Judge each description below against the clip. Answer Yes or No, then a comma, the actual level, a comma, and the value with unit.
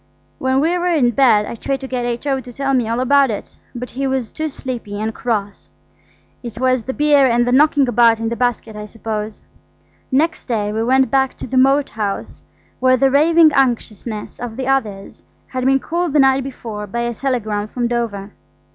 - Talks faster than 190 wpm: Yes, average, 200 wpm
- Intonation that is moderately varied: Yes, average, 3.2 semitones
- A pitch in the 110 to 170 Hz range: No, very high, 250 Hz